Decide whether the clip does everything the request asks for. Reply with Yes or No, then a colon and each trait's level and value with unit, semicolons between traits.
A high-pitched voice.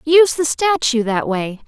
Yes: very high, 270 Hz